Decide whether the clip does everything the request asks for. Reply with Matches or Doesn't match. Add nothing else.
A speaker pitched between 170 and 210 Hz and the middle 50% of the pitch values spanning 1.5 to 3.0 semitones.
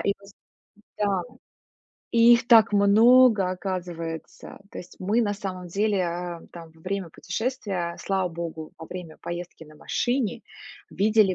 Doesn't match